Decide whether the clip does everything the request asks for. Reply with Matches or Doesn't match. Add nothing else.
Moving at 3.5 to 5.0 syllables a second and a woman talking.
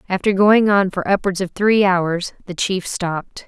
Matches